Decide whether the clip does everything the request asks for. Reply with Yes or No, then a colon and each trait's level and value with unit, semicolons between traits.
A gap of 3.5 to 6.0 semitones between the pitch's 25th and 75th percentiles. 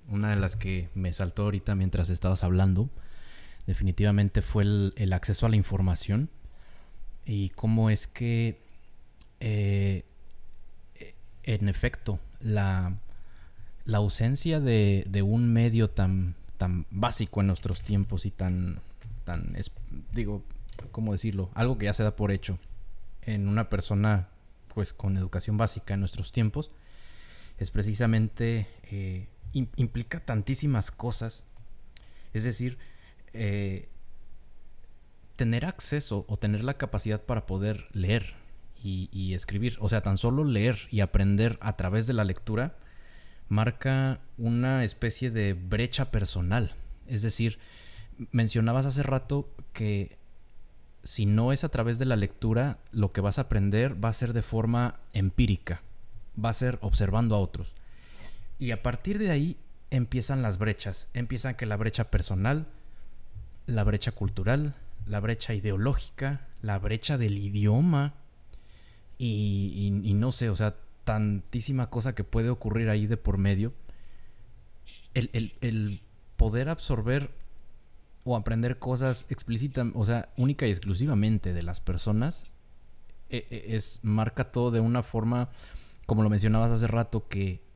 No: average, 3.1 semitones